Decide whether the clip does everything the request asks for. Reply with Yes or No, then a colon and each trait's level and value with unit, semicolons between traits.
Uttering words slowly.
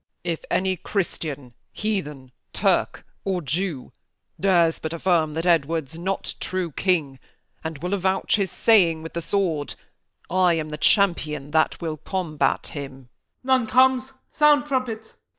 No: average, 150 wpm